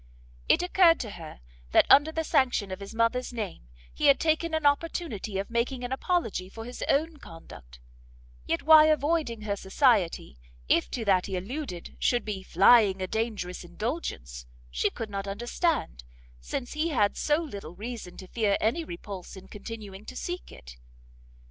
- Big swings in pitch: Yes, wide, 7.2 semitones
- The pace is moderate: Yes, average, 165 wpm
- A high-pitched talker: Yes, high, 225 Hz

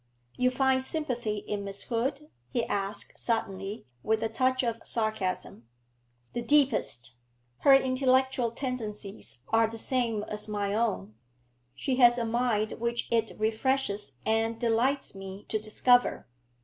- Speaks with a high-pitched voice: Yes, high, 230 Hz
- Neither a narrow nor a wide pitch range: Yes, average, 3.2 semitones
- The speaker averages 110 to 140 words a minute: Yes, slow, 135 wpm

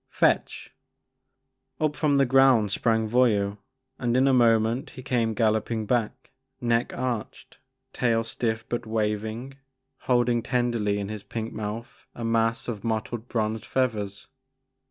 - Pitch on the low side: Yes, low, 115 Hz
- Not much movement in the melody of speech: Yes, narrow, 2.1 semitones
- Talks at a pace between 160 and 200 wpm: No, slow, 135 wpm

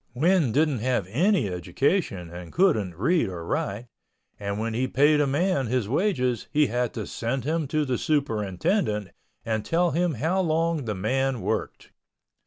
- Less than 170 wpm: Yes, average, 160 wpm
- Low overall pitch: Yes, low, 130 Hz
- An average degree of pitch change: No, wide, 6.7 semitones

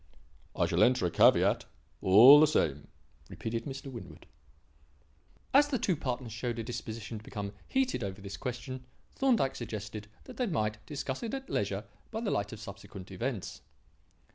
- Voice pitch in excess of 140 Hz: No, low, 115 Hz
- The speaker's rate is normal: Yes, average, 165 wpm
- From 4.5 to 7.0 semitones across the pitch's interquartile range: Yes, average, 5.1 semitones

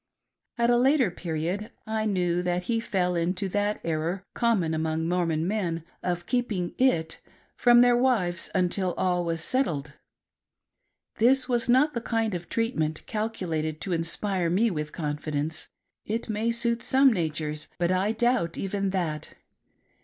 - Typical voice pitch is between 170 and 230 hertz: Yes, medium, 185 Hz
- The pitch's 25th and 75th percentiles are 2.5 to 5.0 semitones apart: No, wide, 5.6 semitones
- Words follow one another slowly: No, average, 145 wpm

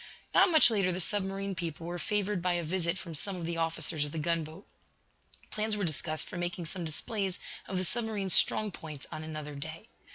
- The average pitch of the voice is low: No, medium, 175 Hz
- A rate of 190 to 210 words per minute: Yes, average, 200 wpm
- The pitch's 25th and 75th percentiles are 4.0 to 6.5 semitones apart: No, average, 3.5 semitones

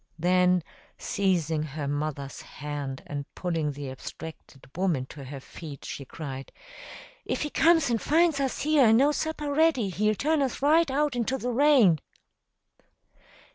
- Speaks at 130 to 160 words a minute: Yes, average, 150 wpm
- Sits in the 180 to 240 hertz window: Yes, medium, 185 Hz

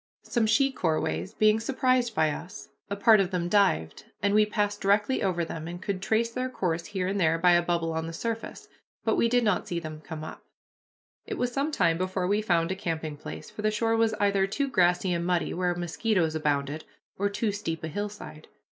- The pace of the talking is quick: Yes, fast, 215 wpm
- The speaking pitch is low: No, high, 190 Hz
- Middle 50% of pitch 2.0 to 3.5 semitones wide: No, average, 4.4 semitones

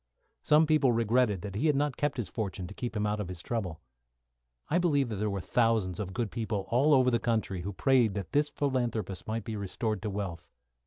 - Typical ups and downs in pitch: Yes, average, 4.4 semitones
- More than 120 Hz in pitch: No, low, 110 Hz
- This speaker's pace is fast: Yes, fast, 215 wpm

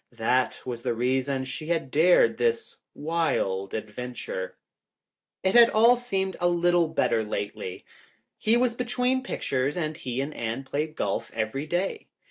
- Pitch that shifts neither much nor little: No, wide, 7.7 semitones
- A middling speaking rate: Yes, average, 145 wpm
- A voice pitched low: No, medium, 155 Hz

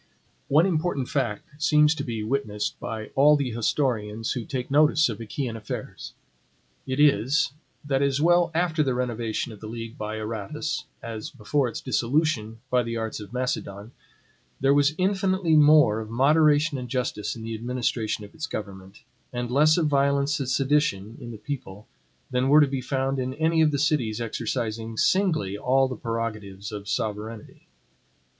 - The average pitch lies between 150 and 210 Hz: No, low, 125 Hz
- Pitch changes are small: No, average, 4.9 semitones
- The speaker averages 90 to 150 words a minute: No, average, 165 wpm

